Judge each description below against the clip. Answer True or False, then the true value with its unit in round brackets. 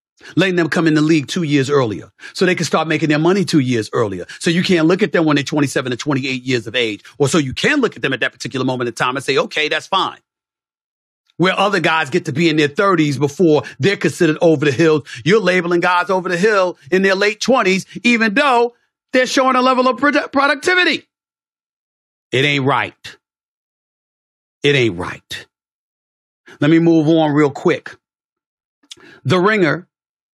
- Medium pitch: True (165 Hz)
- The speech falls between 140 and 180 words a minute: False (200 wpm)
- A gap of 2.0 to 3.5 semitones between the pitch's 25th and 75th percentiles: False (4.7 semitones)